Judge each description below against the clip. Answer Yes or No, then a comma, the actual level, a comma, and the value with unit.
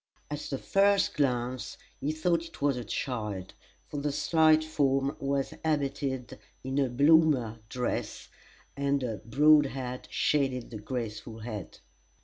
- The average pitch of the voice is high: No, low, 135 Hz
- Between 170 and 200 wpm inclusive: No, slow, 135 wpm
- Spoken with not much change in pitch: No, average, 3.4 semitones